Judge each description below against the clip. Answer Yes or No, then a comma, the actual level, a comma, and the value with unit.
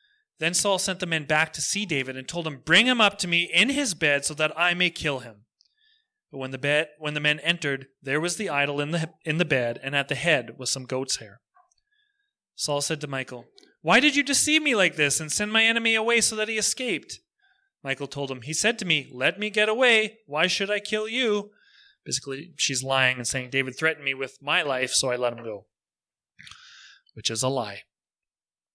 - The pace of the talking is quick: Yes, fast, 225 wpm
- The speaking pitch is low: No, medium, 160 Hz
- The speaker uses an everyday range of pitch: No, wide, 8.0 semitones